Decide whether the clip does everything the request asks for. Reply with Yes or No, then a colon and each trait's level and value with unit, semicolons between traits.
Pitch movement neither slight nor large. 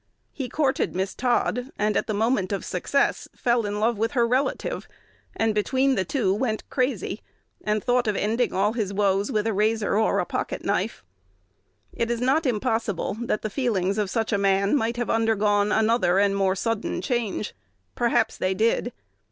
Yes: average, 3.0 semitones